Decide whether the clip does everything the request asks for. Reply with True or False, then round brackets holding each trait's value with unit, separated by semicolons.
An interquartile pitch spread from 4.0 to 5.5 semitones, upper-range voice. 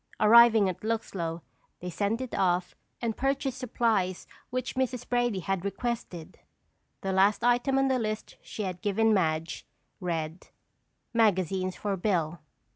True (4.6 semitones; 205 Hz)